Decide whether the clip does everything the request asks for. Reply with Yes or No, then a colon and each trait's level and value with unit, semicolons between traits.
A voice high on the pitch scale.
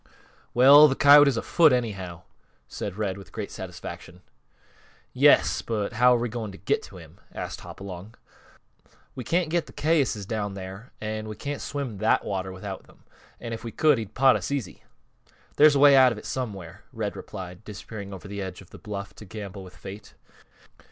No: low, 110 Hz